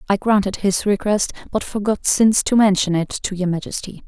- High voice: Yes, high, 200 Hz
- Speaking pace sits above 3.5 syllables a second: Yes, 5.4 syllables/s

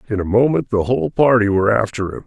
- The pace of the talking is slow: No, fast, 240 wpm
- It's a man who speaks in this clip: Yes, male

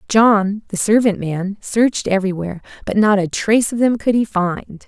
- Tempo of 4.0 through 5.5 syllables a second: Yes, 5.0 syllables/s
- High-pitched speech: Yes, high, 205 Hz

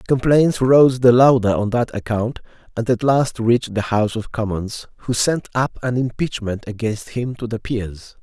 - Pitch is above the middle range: No, low, 120 Hz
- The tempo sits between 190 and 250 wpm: No, average, 180 wpm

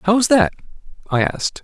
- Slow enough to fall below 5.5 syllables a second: No, 5.6 syllables/s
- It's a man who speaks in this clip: Yes, male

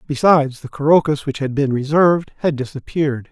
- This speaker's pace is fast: No, average, 165 wpm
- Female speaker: No, male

